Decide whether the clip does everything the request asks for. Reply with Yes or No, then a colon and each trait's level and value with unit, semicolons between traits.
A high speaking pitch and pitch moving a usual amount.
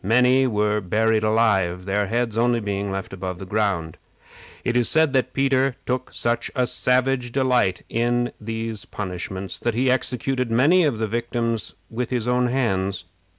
No: low, 115 Hz; average, 3.5 semitones